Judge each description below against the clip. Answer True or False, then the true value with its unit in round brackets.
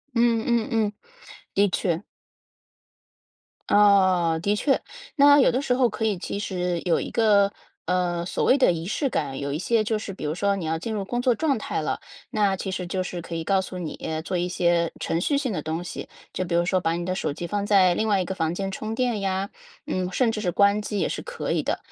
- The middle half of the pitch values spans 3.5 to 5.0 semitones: True (3.8 semitones)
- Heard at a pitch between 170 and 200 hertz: True (195 Hz)